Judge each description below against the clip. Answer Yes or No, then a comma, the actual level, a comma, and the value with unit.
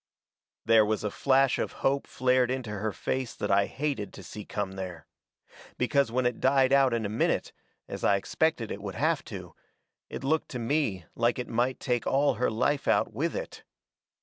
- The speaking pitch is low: Yes, low, 125 Hz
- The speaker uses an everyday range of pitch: Yes, average, 4.1 semitones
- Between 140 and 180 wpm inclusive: No, average, 195 wpm